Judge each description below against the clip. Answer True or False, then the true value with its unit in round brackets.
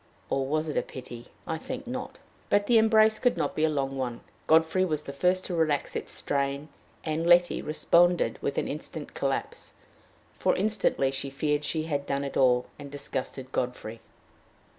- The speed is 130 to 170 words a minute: False (180 wpm)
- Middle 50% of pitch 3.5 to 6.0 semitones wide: True (4.3 semitones)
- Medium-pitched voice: True (150 Hz)